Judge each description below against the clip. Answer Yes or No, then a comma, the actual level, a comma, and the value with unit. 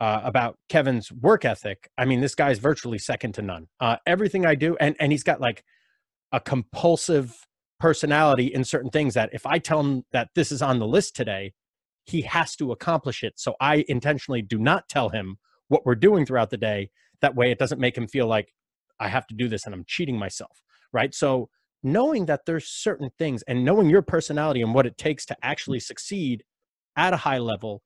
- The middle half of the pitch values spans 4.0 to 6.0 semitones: Yes, average, 4.6 semitones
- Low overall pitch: Yes, low, 130 Hz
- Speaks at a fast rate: Yes, fast, 220 wpm